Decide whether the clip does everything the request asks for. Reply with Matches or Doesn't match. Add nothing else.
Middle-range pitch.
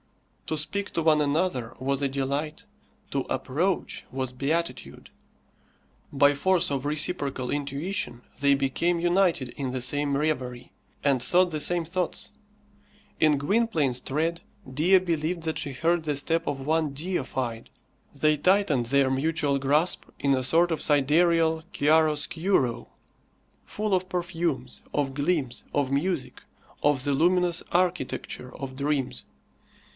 Matches